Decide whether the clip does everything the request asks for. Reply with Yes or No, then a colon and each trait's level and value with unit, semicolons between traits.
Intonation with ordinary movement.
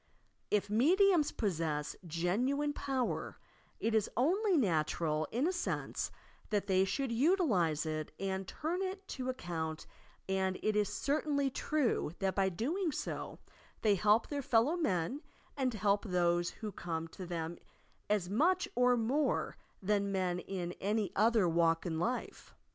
No: wide, 7.7 semitones